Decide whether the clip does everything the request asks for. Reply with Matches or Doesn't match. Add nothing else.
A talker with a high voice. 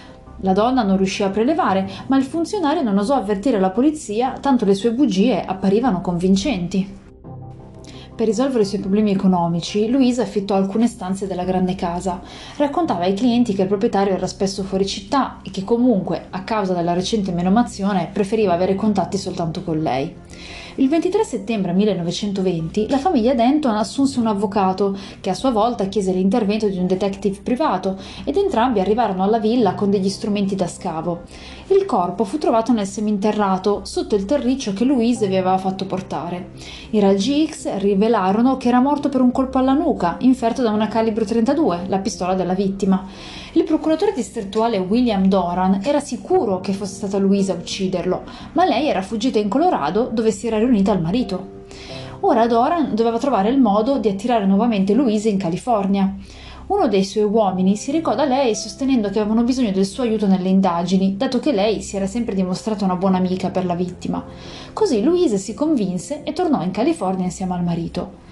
Matches